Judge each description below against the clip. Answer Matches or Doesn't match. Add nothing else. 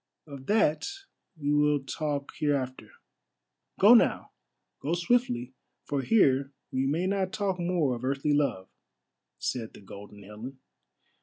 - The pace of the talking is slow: Matches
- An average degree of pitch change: Matches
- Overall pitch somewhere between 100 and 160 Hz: Matches